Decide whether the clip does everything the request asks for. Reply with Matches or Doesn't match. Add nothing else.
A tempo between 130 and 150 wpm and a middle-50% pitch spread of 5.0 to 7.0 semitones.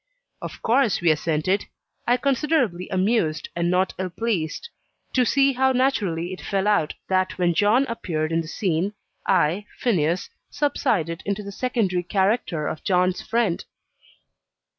Matches